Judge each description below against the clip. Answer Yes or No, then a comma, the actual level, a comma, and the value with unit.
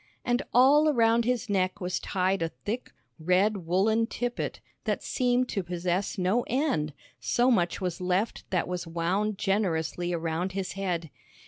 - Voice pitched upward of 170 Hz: Yes, high, 190 Hz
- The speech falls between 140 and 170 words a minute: Yes, average, 150 wpm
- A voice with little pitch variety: No, average, 4.5 semitones